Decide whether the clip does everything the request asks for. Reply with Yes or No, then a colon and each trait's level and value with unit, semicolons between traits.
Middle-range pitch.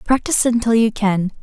No: high, 220 Hz